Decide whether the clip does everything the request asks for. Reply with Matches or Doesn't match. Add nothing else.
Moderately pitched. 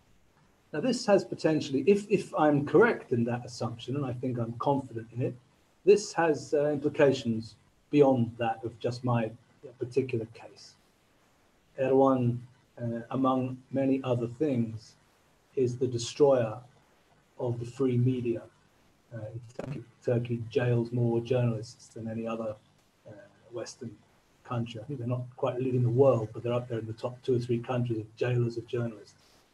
Doesn't match